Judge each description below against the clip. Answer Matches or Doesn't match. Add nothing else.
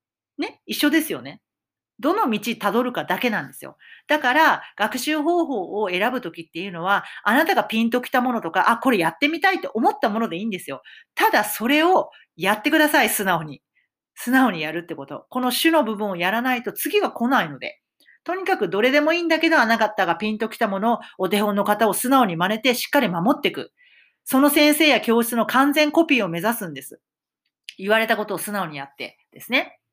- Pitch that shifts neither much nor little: Doesn't match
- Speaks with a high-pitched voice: Matches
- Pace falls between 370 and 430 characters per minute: Matches